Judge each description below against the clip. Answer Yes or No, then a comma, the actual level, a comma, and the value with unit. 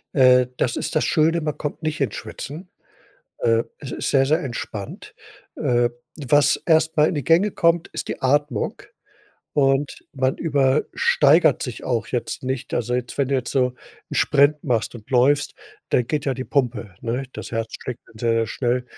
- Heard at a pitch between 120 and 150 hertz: Yes, low, 135 Hz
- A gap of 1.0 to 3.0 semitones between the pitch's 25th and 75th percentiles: No, average, 3.4 semitones